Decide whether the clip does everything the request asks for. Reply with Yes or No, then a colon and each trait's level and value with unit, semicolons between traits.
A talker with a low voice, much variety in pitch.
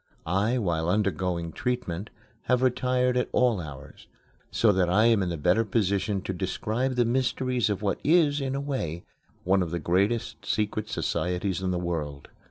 Yes: low, 100 Hz; wide, 5.8 semitones